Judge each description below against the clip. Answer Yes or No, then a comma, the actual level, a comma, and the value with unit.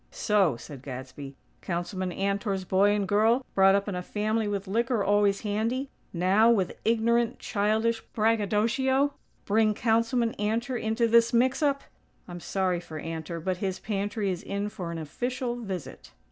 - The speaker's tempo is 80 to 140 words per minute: No, average, 155 wpm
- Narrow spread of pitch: No, average, 3.6 semitones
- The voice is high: Yes, high, 210 Hz